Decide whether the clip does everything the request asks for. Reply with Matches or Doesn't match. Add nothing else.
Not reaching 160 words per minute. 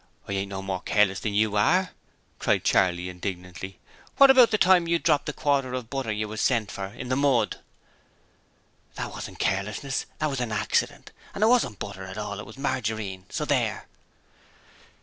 Doesn't match